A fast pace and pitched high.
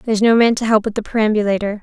Yes: fast, 265 wpm; high, 215 Hz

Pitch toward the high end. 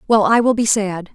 Yes: high, 210 Hz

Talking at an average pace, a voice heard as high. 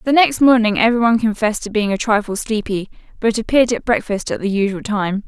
No: fast, 215 wpm; high, 220 Hz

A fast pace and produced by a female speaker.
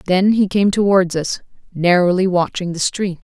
No: average, 165 wpm; female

